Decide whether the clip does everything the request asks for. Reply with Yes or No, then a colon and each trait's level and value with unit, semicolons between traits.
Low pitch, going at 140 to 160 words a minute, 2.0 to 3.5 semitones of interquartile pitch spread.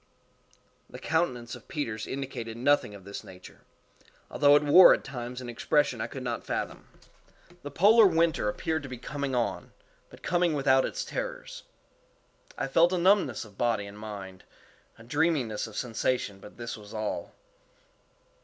No: low, 125 Hz; average, 155 wpm; average, 5.2 semitones